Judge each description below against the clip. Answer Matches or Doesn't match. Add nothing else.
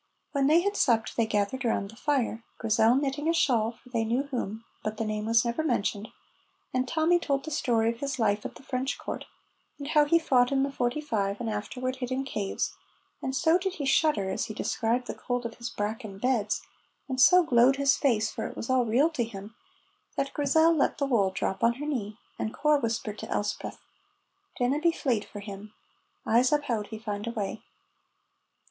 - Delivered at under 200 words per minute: Doesn't match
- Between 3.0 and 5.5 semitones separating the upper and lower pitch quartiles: Matches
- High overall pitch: Matches